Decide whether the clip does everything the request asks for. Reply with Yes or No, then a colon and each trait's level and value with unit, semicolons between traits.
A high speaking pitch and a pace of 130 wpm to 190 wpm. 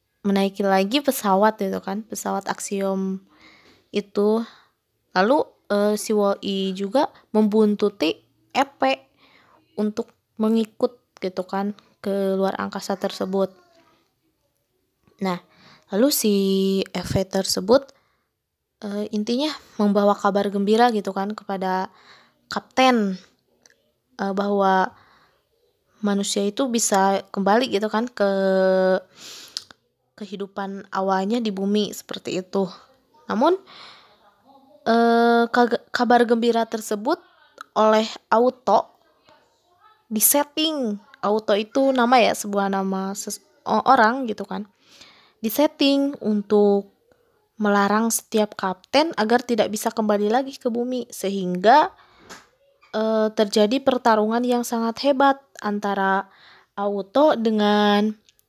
No: high, 210 Hz; average, 95 wpm